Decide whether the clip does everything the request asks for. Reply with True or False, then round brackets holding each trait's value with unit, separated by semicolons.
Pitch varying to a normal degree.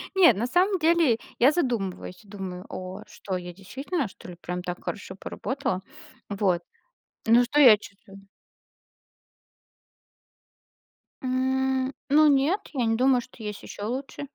False (5.8 semitones)